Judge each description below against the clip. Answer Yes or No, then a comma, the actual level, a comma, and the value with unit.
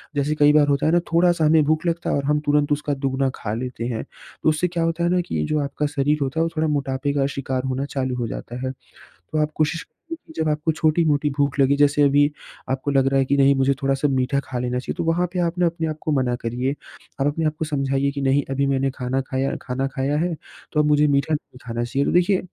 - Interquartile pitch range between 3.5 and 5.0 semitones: No, narrow, 2.5 semitones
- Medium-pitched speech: Yes, medium, 145 Hz